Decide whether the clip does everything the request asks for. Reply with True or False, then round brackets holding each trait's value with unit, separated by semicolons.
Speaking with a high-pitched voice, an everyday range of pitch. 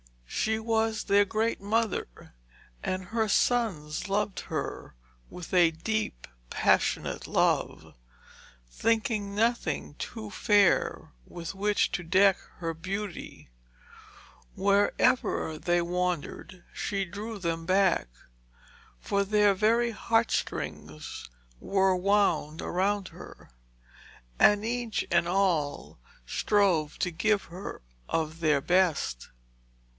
True (195 Hz; 3.7 semitones)